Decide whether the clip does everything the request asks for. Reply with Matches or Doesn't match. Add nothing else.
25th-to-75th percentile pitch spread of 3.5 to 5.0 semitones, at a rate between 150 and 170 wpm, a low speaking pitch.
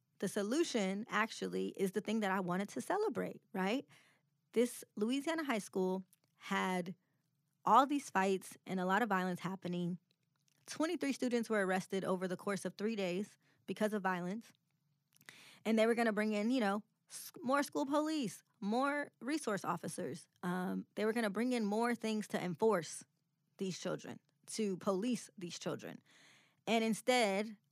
Doesn't match